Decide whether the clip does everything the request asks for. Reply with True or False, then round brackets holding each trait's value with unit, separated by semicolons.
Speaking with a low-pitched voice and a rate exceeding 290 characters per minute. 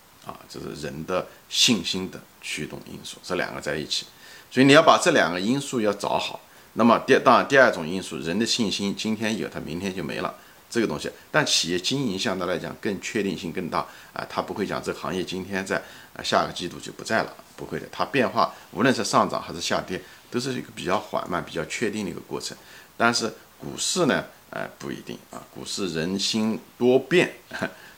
True (100 Hz; 315 characters per minute)